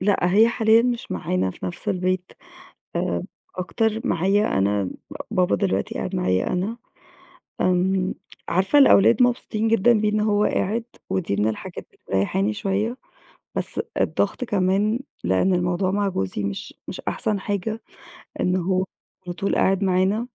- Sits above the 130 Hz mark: Yes, high, 190 Hz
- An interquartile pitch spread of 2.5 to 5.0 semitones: Yes, average, 3.1 semitones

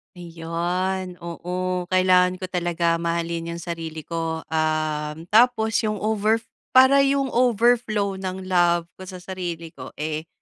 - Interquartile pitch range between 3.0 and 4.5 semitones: No, narrow, 2.4 semitones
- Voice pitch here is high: No, medium, 180 Hz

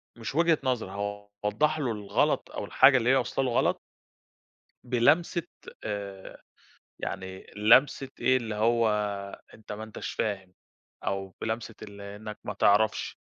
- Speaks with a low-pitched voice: Yes, low, 110 Hz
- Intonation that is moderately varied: Yes, average, 3.6 semitones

